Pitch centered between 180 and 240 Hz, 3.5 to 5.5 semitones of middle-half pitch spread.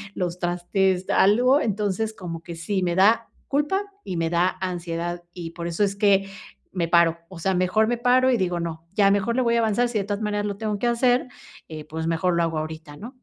Yes: high, 190 Hz; average, 4.2 semitones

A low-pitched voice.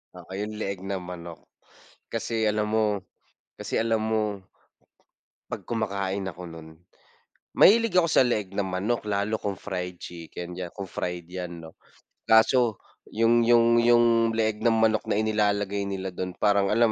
Yes: low, 105 Hz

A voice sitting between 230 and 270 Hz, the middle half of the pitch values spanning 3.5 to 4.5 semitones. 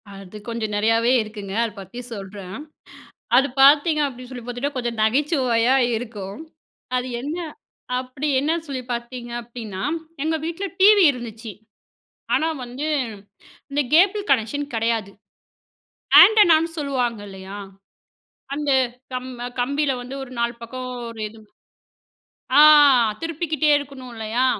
Yes: very high, 250 Hz; average, 4.2 semitones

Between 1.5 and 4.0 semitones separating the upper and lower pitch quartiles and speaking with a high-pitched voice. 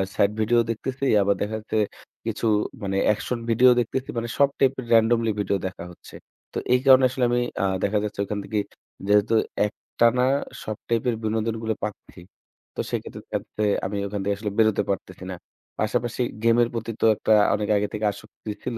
No: narrow, 2.4 semitones; low, 110 Hz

